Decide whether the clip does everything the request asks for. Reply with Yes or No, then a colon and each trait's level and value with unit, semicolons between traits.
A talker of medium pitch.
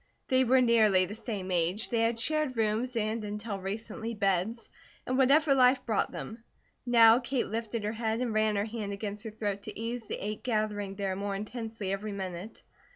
No: high, 220 Hz